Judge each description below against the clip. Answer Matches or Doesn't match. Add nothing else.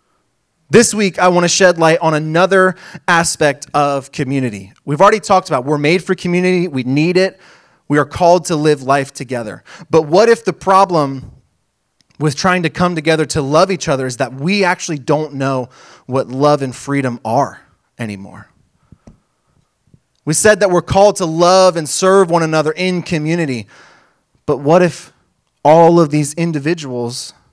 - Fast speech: Doesn't match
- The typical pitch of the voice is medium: Matches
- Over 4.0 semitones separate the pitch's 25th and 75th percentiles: Matches